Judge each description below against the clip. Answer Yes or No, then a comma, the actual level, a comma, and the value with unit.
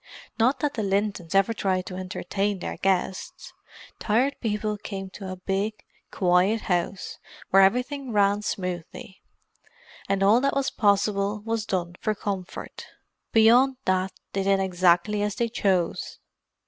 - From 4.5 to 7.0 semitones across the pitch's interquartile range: No, average, 2.7 semitones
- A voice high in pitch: Yes, high, 200 Hz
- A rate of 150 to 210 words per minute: No, average, 140 wpm